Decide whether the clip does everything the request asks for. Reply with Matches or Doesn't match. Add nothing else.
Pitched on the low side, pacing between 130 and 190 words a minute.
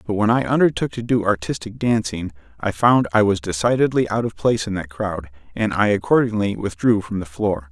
Doesn't match